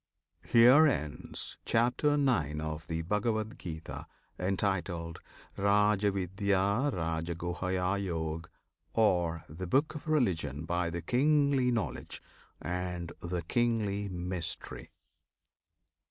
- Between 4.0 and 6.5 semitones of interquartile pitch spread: Yes, average, 5.1 semitones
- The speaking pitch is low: Yes, very low, 95 Hz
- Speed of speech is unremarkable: No, slow, 85 wpm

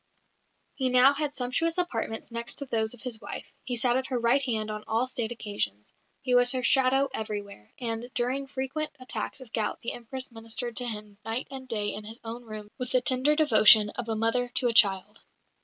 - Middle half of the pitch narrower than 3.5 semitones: Yes, average, 2.8 semitones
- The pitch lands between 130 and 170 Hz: No, high, 240 Hz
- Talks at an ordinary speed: No, fast, 210 wpm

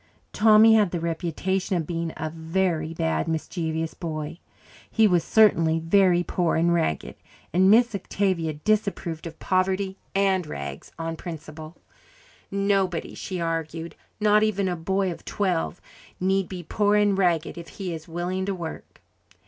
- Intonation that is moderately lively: Yes, average, 3.1 semitones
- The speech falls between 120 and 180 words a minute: Yes, average, 150 wpm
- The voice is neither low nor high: Yes, medium, 175 Hz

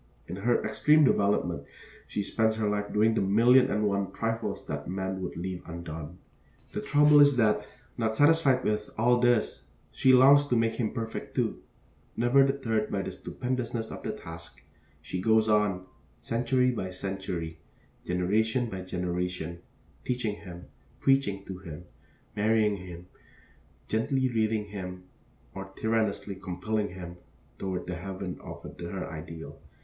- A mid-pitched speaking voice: No, low, 105 Hz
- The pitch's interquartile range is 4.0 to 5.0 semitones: Yes, average, 4.3 semitones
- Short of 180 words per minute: Yes, average, 145 wpm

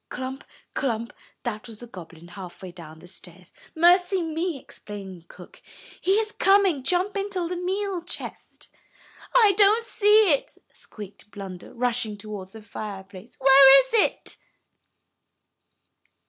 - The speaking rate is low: Yes, slow, 130 wpm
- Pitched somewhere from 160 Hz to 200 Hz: No, very high, 260 Hz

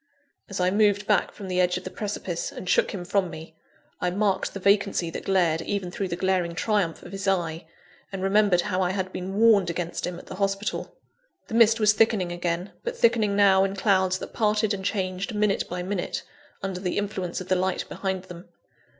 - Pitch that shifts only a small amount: Yes, narrow, 2.2 semitones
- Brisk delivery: Yes, fast, 210 wpm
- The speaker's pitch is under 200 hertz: Yes, high, 190 Hz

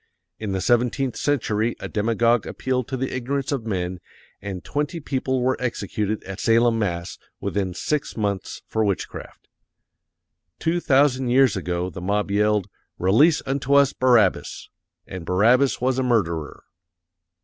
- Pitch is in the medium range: No, low, 115 Hz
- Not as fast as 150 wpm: Yes, average, 140 wpm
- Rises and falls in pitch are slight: No, average, 4.8 semitones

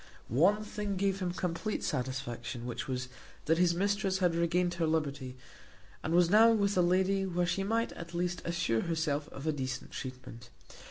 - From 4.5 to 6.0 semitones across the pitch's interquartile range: Yes, average, 5.3 semitones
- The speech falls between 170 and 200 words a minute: Yes, average, 175 wpm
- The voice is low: No, medium, 170 Hz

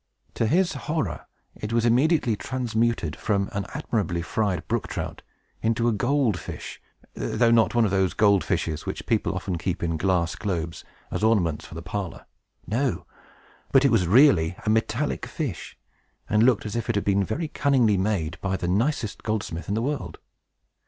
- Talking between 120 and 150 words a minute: No, average, 175 wpm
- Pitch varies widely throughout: No, average, 4.5 semitones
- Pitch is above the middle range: No, low, 105 Hz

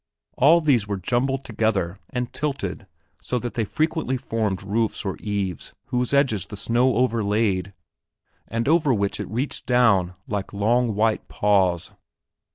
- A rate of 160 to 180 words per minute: No, average, 145 wpm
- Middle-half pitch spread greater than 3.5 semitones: Yes, average, 3.9 semitones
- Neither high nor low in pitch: No, low, 115 Hz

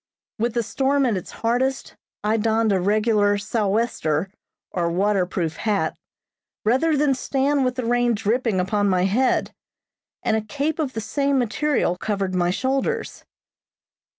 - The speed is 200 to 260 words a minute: No, average, 150 wpm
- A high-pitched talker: Yes, high, 225 Hz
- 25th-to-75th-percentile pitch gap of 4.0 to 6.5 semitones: Yes, average, 4.6 semitones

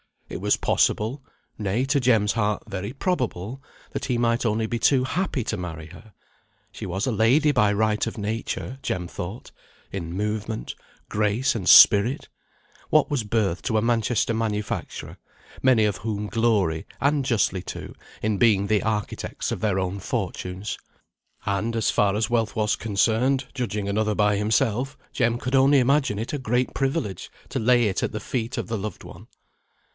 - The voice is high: No, low, 110 Hz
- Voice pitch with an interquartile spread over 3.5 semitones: No, average, 3.2 semitones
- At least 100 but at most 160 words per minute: No, average, 170 wpm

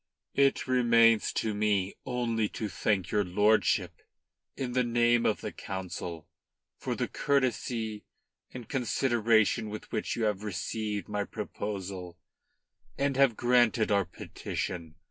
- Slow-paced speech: Yes, slow, 125 wpm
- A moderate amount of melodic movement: Yes, average, 3.0 semitones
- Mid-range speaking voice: No, low, 110 Hz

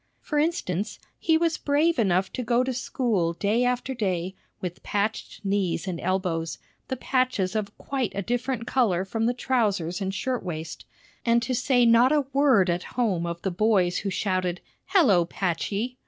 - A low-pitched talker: No, high, 215 Hz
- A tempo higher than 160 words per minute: Yes, average, 170 wpm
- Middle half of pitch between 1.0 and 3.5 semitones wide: No, wide, 5.5 semitones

